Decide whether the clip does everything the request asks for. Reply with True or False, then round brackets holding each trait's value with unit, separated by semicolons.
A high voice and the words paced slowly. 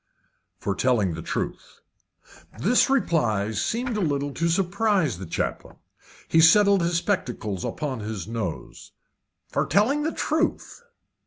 False (160 Hz; 130 wpm)